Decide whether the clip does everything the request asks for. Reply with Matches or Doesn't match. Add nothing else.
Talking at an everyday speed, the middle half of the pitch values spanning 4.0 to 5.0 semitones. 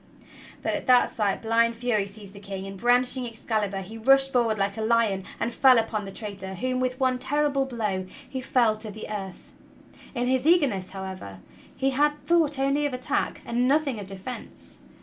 Matches